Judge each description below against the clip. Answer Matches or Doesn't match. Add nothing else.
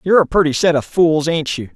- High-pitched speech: Doesn't match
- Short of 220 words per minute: Doesn't match